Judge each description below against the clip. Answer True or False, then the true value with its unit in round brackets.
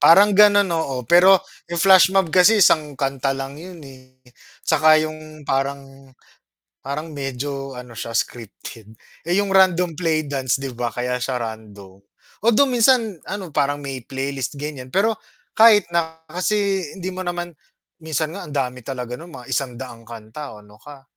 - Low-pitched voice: False (145 Hz)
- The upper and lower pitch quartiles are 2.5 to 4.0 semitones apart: False (5.3 semitones)